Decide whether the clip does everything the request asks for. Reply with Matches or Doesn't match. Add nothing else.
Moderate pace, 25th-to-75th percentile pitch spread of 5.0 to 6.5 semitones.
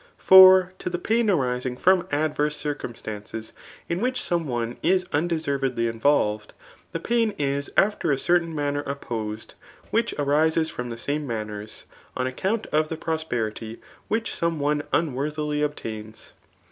Matches